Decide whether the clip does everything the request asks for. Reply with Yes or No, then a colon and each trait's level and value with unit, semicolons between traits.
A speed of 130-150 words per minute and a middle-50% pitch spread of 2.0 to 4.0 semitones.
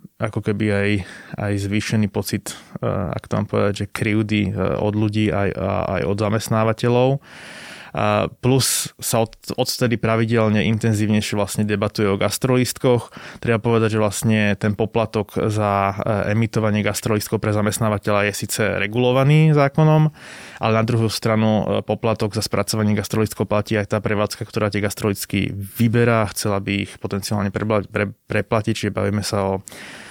No: average, 135 wpm; narrow, 1.6 semitones